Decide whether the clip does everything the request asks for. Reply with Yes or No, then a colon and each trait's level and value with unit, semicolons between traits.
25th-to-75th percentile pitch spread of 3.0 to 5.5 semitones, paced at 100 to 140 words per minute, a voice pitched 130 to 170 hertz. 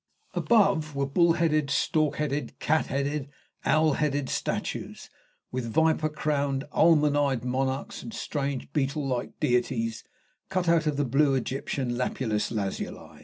No: narrow, 2.6 semitones; slow, 135 wpm; medium, 140 Hz